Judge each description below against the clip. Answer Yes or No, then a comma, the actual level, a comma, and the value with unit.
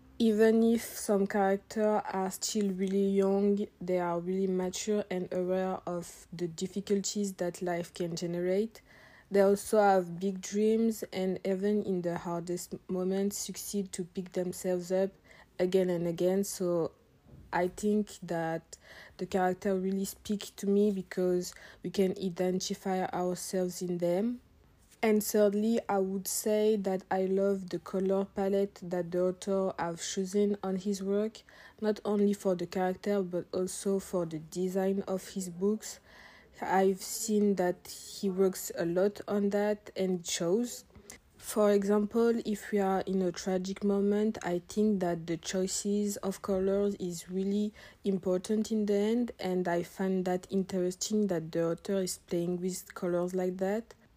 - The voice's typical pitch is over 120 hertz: Yes, high, 190 Hz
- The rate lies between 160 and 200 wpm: No, average, 150 wpm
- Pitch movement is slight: Yes, narrow, 1.9 semitones